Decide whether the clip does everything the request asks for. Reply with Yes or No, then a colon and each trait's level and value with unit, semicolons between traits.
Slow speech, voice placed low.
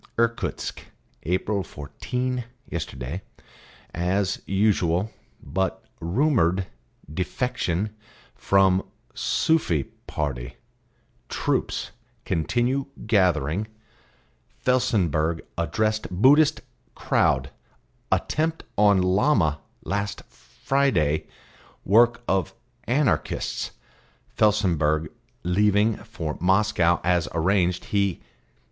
Yes: slow, 70 wpm; very low, 95 Hz